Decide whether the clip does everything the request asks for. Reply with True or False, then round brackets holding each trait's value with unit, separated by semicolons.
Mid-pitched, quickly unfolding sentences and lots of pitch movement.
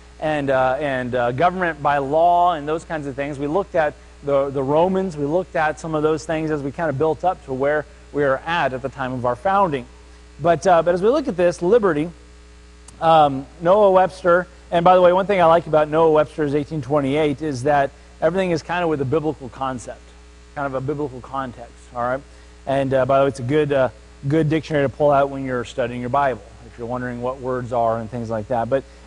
False (145 Hz; 235 wpm; 4.0 semitones)